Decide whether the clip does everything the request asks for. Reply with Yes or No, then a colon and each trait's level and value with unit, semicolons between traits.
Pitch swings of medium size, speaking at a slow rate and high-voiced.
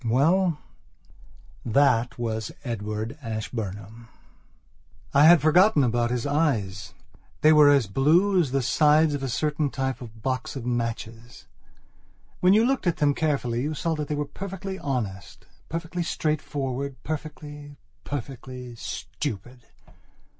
No: average, 4.7 semitones; slow, 130 wpm; low, 135 Hz